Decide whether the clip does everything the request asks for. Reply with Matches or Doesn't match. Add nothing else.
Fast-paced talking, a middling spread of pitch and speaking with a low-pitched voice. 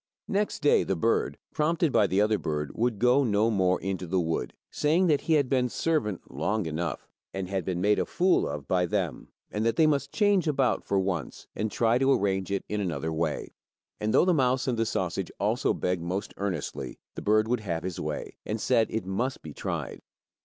Doesn't match